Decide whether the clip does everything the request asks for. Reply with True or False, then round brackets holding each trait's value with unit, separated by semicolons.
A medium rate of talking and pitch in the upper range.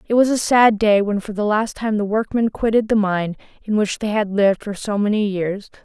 False (245 wpm; 210 Hz)